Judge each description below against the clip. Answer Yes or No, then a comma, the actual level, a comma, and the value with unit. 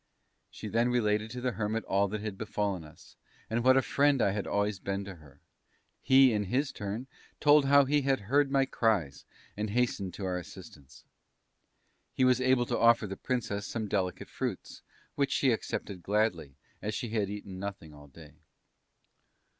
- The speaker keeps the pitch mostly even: No, average, 4.5 semitones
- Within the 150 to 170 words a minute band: No, average, 180 wpm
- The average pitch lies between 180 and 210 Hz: No, low, 105 Hz